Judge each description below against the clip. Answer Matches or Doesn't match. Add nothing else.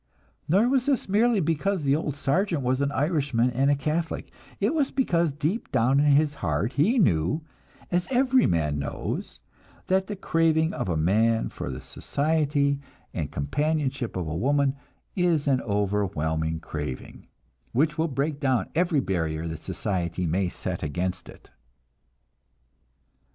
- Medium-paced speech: Matches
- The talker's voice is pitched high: Doesn't match